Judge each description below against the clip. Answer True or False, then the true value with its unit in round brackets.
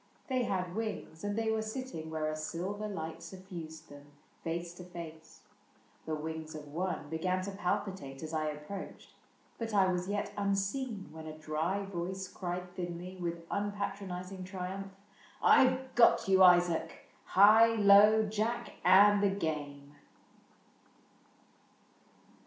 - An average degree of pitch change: True (4.0 semitones)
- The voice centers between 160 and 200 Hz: True (185 Hz)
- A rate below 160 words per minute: True (140 wpm)